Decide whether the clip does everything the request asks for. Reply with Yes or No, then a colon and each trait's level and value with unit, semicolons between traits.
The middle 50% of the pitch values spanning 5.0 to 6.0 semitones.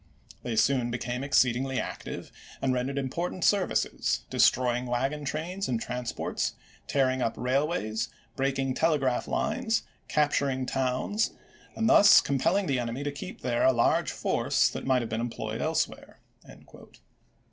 No: average, 3.0 semitones